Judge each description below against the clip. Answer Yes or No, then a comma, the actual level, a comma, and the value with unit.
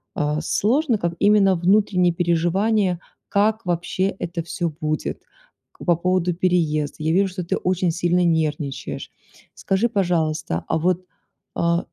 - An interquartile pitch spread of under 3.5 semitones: Yes, average, 2.7 semitones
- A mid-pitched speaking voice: Yes, medium, 175 Hz